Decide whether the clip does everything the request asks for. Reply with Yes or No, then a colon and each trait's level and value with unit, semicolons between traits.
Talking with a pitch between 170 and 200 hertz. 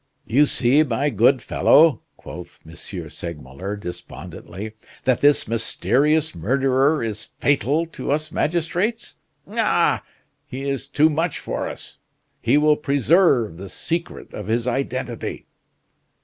No: low, 135 Hz